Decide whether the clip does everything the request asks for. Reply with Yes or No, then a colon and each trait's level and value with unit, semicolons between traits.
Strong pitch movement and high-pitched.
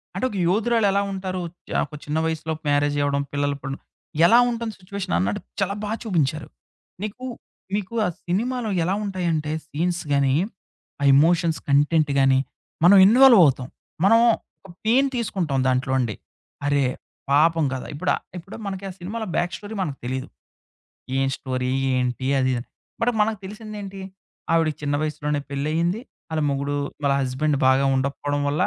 No: wide, 5.9 semitones; medium, 160 Hz